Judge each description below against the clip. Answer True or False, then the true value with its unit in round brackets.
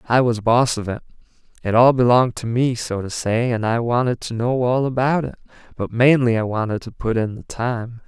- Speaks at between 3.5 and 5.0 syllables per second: False (5.3 syllables/s)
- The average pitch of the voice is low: True (120 Hz)